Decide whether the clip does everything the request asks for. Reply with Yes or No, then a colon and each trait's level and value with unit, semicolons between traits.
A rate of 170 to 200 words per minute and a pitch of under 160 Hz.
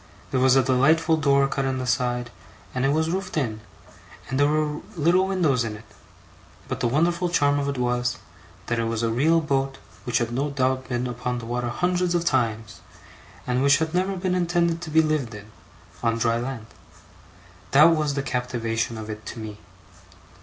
Yes: average, 195 wpm; low, 135 Hz